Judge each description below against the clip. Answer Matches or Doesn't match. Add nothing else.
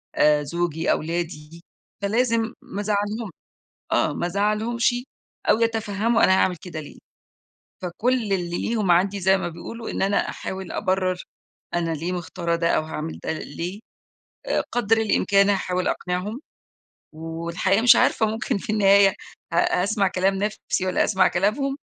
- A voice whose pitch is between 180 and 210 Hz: Matches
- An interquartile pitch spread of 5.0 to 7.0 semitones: Doesn't match